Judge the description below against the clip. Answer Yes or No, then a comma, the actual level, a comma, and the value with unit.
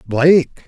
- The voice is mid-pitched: Yes, medium, 145 Hz